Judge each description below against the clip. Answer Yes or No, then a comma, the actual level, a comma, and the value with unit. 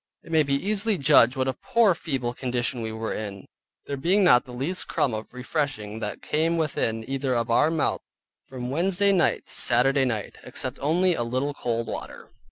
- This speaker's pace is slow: No, average, 190 wpm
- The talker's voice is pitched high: No, low, 135 Hz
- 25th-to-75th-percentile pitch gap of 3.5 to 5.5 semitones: Yes, average, 5.1 semitones